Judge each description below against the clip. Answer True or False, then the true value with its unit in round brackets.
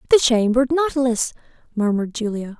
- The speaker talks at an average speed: False (115 wpm)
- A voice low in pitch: False (240 Hz)